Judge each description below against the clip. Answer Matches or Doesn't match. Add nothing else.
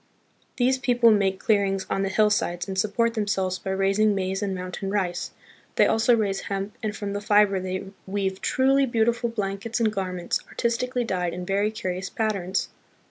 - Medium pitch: Doesn't match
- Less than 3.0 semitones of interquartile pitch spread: Matches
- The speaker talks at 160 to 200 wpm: Matches